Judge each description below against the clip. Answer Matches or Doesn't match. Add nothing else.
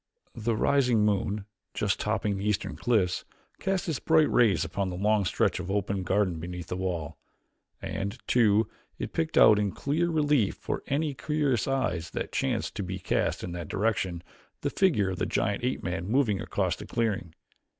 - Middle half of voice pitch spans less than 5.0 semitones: Doesn't match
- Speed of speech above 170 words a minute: Matches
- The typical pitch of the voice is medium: Doesn't match